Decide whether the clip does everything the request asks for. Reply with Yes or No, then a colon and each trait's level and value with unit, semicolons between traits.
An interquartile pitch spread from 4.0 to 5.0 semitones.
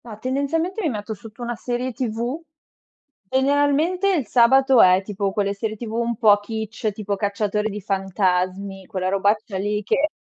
Yes: average, 4.3 semitones